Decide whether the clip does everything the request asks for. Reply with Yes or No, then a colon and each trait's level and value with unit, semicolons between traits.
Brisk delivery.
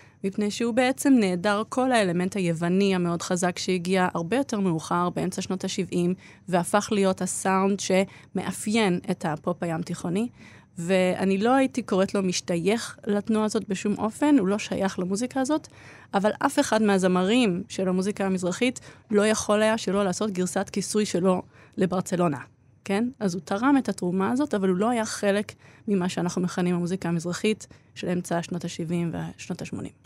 Yes: fast, 155 wpm